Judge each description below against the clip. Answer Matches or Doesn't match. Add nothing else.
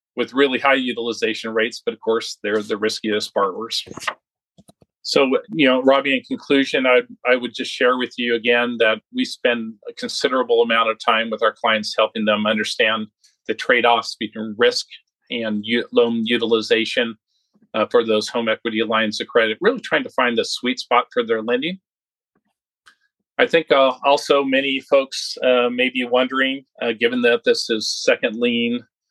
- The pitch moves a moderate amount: Matches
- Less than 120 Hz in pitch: Doesn't match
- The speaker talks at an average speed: Matches